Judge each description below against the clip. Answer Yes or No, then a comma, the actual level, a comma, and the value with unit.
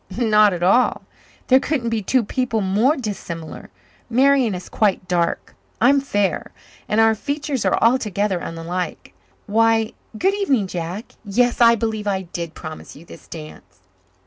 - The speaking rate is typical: Yes, average, 150 wpm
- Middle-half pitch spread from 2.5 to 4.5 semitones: No, average, 5.2 semitones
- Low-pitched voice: No, high, 215 Hz